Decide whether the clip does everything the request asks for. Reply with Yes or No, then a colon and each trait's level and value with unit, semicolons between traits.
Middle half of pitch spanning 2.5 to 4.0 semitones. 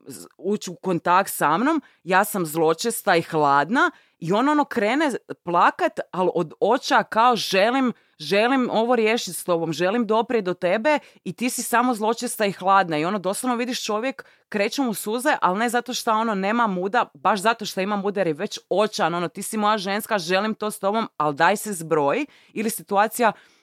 No: average, 4.4 semitones